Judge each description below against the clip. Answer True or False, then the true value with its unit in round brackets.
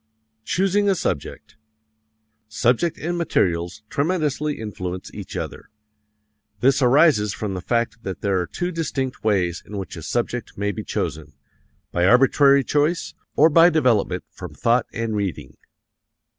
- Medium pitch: False (120 Hz)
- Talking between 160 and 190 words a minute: False (140 wpm)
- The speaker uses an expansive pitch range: True (7.4 semitones)